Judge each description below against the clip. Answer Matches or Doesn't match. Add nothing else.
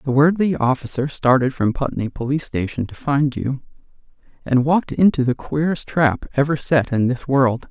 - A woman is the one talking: Doesn't match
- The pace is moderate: Matches